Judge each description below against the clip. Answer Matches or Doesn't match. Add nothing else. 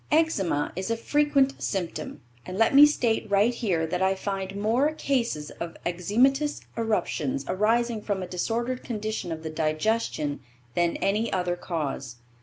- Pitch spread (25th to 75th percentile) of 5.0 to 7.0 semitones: Matches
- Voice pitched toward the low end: Doesn't match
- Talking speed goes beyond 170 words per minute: Doesn't match